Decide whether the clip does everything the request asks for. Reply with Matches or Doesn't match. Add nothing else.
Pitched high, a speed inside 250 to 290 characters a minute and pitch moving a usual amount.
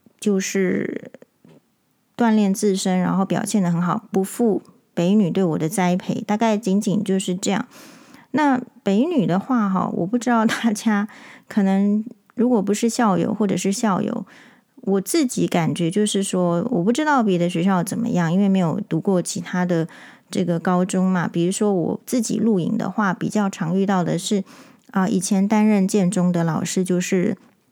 Matches